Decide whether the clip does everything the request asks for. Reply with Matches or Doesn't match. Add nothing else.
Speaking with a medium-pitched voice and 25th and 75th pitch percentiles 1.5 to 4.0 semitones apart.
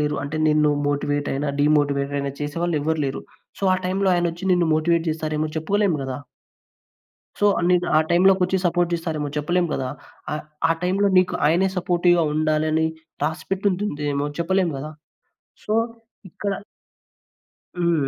Matches